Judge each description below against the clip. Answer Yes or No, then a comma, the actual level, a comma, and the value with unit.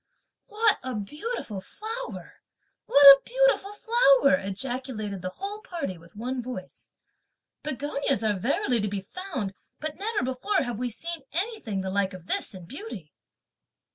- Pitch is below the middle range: No, very high, 260 Hz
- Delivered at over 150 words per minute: No, average, 145 wpm